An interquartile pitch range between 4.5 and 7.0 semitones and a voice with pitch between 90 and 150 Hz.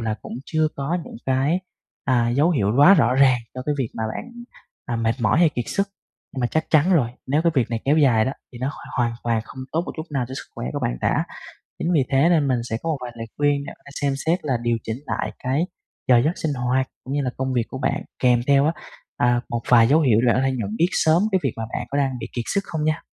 No: average, 4.1 semitones; low, 135 Hz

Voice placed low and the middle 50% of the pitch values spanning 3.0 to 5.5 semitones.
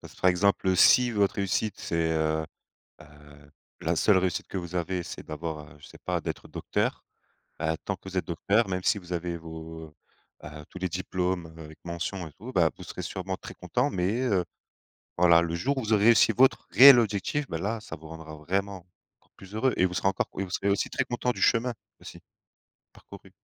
Yes: very low, 90 Hz; average, 3.6 semitones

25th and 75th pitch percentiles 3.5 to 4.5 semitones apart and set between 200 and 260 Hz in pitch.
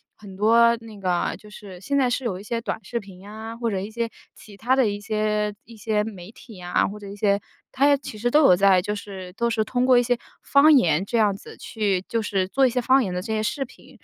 No: average, 3.0 semitones; high, 215 Hz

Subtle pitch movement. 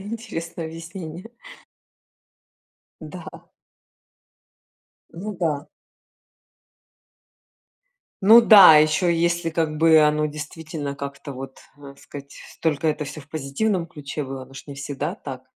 No: average, 3.1 semitones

